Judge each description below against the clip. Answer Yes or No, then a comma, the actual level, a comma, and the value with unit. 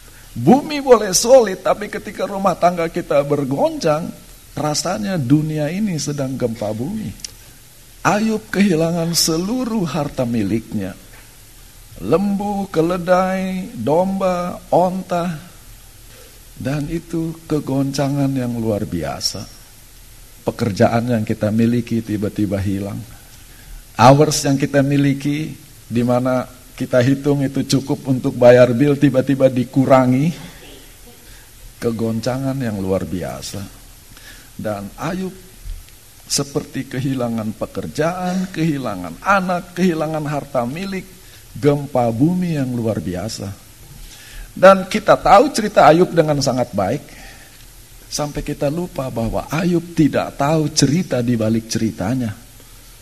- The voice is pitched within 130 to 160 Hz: Yes, low, 135 Hz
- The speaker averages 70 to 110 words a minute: Yes, average, 100 wpm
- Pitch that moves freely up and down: Yes, wide, 6.3 semitones